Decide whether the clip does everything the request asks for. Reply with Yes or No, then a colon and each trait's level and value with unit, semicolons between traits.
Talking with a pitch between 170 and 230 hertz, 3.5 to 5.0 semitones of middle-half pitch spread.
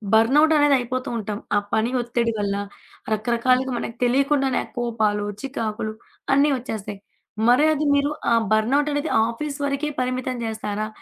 No: high, 245 Hz; average, 4.1 semitones